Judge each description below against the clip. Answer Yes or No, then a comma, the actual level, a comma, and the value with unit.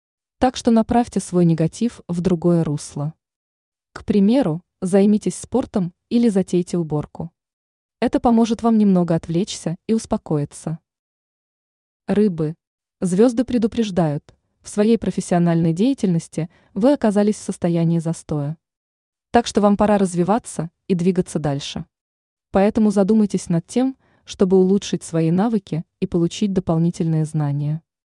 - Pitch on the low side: No, high, 190 Hz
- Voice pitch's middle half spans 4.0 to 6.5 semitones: Yes, average, 4.5 semitones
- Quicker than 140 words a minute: No, average, 115 wpm